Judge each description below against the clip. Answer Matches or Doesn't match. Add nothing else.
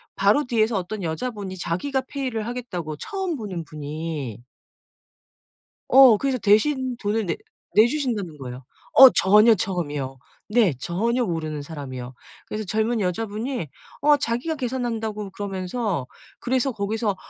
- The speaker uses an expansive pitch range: Matches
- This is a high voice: Matches